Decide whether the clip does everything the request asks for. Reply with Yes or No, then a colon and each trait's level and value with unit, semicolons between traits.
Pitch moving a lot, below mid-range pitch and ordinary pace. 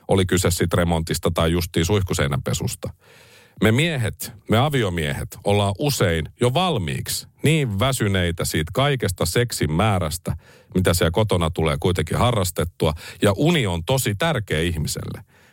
Yes: wide, 6.2 semitones; low, 100 Hz; average, 130 wpm